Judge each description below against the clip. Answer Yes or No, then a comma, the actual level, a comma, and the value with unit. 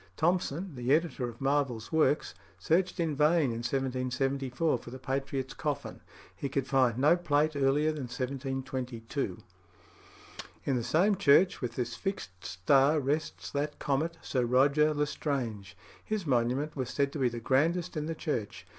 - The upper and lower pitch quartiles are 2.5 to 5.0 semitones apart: Yes, average, 3.3 semitones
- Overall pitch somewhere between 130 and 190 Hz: Yes, low, 135 Hz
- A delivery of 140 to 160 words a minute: Yes, average, 155 wpm